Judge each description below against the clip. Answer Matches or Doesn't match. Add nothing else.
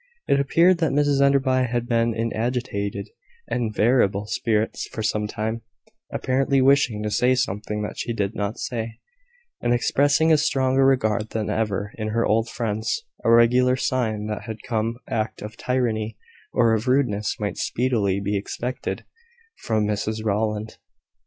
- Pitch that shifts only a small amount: Doesn't match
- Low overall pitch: Matches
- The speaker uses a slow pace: Doesn't match